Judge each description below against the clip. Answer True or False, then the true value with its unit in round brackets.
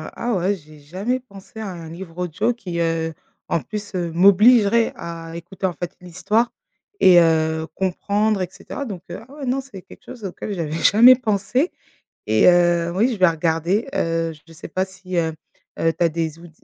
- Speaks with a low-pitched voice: False (180 Hz)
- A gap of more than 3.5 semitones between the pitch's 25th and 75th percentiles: True (4.1 semitones)